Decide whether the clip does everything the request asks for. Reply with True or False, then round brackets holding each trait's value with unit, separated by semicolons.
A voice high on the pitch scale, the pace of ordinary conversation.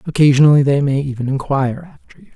False (140 Hz; 180 wpm)